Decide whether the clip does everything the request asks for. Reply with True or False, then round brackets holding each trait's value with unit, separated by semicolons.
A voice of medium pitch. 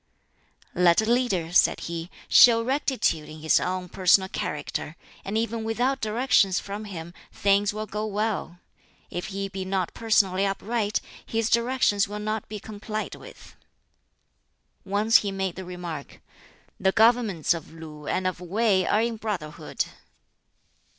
False (200 Hz)